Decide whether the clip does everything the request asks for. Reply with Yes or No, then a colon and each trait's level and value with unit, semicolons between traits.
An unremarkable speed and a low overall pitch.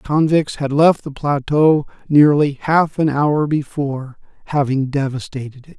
No: average, 145 wpm; medium, 145 Hz